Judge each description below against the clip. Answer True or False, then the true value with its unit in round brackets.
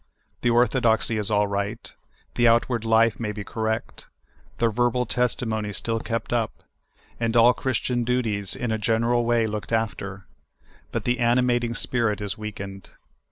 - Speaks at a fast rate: False (160 wpm)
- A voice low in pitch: True (115 Hz)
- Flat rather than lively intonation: True (2.1 semitones)